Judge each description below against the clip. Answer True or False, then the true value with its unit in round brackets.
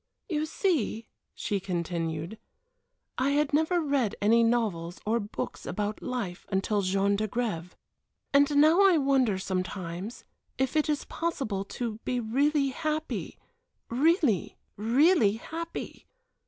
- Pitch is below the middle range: False (235 Hz)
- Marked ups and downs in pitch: True (6.9 semitones)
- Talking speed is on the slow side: True (120 wpm)